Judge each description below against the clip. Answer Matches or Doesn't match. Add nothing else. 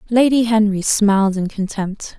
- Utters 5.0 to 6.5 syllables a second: Doesn't match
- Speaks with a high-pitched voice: Matches